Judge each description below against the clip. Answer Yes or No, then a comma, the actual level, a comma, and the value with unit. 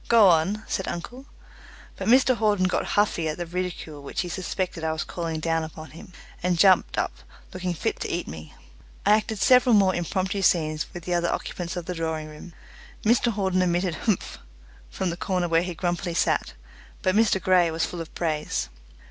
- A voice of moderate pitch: Yes, medium, 180 Hz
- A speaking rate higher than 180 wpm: Yes, average, 190 wpm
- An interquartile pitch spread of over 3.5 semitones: No, average, 2.8 semitones